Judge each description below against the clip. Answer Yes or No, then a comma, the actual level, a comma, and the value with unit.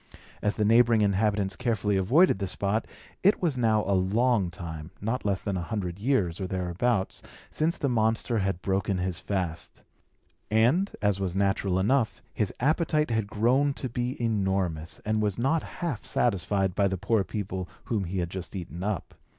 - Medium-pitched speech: No, low, 105 Hz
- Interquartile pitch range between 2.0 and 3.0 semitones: No, average, 3.8 semitones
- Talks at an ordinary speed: Yes, average, 175 wpm